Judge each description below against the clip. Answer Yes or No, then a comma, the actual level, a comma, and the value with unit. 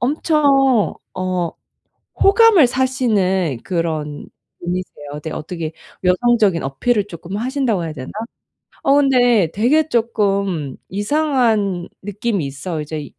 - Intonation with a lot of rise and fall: Yes, wide, 6.6 semitones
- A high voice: Yes, high, 200 Hz